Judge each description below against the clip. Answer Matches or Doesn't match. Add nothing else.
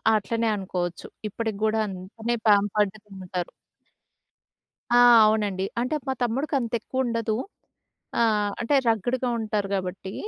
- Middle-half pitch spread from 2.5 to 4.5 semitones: Matches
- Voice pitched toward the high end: Matches